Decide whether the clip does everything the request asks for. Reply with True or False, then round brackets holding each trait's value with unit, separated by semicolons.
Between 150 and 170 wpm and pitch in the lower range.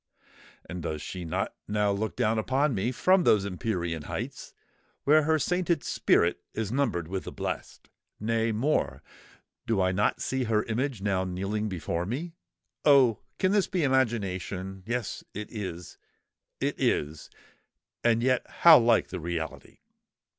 False (140 wpm; 110 Hz)